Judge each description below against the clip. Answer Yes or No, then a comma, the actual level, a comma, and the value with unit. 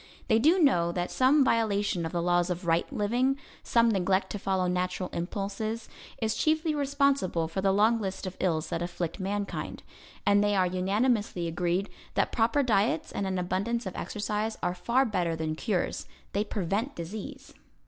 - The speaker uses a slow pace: No, average, 170 wpm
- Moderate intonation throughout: Yes, average, 4.1 semitones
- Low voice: No, high, 200 Hz